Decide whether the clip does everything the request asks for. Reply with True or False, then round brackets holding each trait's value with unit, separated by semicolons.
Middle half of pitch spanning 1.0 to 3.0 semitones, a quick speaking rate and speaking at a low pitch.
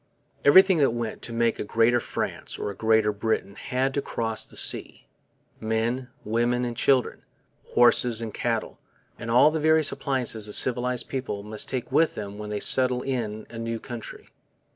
False (2.6 semitones; 170 wpm; 120 Hz)